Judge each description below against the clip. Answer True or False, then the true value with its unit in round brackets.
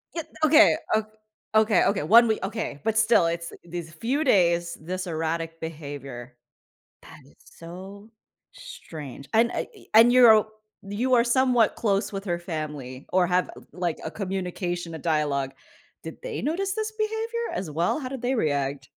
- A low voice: False (185 Hz)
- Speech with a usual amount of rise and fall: False (6.4 semitones)